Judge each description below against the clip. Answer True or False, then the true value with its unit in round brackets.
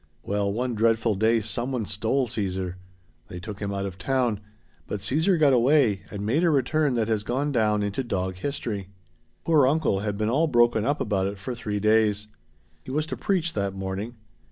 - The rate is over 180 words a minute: True (190 wpm)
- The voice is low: True (110 Hz)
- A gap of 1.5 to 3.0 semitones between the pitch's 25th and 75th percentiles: False (4.6 semitones)